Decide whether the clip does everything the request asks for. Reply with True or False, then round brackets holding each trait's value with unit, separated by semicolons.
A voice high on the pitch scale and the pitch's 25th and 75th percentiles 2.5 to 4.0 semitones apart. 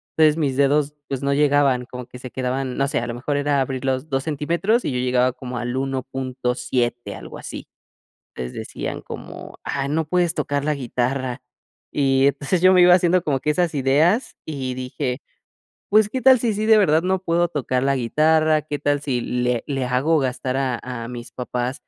False (135 Hz; 3.5 semitones)